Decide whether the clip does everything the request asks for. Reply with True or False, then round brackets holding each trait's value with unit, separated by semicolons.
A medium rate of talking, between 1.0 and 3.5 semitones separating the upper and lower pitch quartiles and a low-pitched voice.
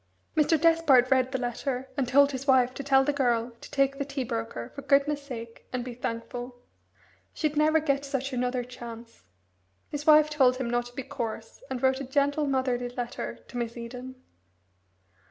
False (185 wpm; 2.5 semitones; 260 Hz)